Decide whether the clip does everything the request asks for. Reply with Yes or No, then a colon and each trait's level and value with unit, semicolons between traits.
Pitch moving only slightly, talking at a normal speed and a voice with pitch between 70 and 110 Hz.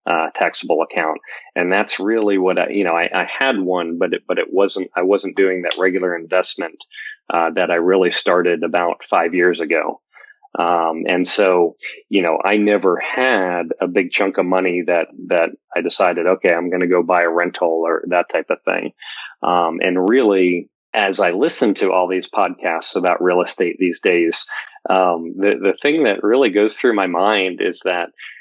Yes: narrow, 1.6 semitones; average, 190 wpm; very low, 90 Hz